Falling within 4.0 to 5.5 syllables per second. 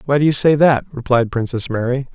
No: 5.7 syllables/s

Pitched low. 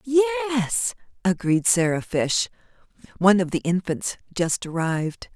No: medium, 185 Hz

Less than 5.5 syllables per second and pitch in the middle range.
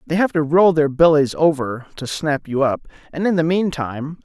Yes: 5.1 syllables/s; medium, 155 Hz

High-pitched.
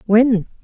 Yes: high, 220 Hz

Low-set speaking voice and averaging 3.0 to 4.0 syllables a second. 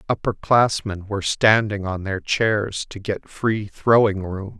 Yes: low, 105 Hz; 3.9 syllables/s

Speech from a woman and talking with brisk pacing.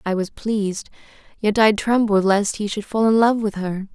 Yes: female; fast, 215 wpm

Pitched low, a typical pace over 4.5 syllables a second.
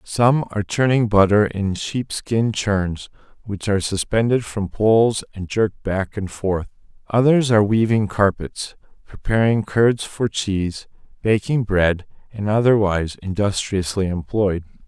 No: low, 105 Hz; 4.3 syllables/s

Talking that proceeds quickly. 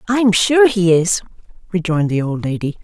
No: average, 170 wpm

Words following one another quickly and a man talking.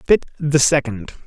No: average, 145 wpm; male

